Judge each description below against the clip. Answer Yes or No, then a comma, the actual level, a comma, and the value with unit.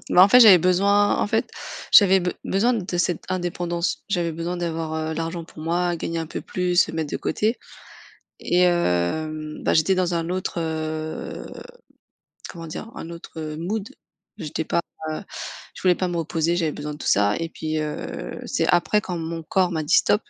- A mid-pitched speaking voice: Yes, medium, 170 Hz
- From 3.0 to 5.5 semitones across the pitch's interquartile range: No, narrow, 2.4 semitones